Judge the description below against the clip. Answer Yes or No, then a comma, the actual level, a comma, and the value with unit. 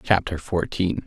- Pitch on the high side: No, very low, 90 Hz